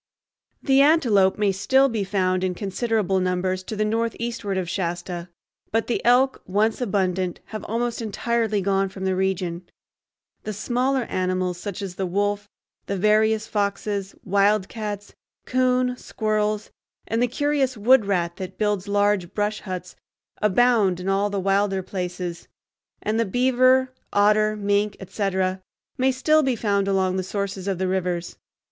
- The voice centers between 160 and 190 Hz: No, high, 205 Hz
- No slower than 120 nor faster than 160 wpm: Yes, average, 150 wpm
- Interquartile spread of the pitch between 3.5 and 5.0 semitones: No, average, 3.1 semitones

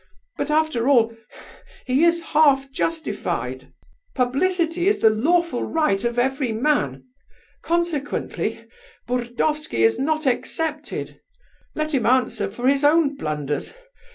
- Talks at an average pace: No, slow, 115 wpm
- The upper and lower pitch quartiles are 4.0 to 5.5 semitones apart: Yes, average, 4.6 semitones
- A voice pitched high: Yes, very high, 275 Hz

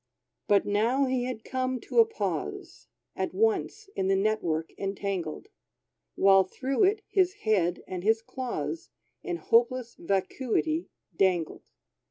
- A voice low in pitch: No, high, 220 Hz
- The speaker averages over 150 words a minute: No, slow, 135 wpm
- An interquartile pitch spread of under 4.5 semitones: No, wide, 5.6 semitones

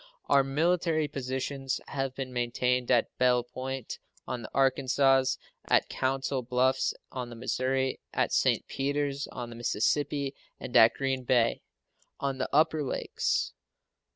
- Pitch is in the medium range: No, low, 130 Hz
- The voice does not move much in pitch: Yes, narrow, 1.6 semitones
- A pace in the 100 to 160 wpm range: Yes, slow, 135 wpm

